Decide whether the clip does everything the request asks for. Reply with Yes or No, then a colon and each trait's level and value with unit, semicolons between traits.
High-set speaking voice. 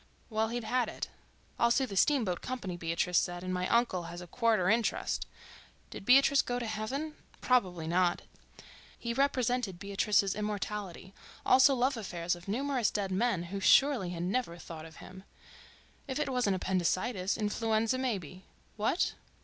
Yes: high, 210 Hz